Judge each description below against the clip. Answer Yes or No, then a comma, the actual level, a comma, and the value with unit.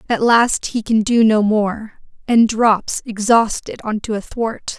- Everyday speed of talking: Yes, average, 175 wpm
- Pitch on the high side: Yes, high, 220 Hz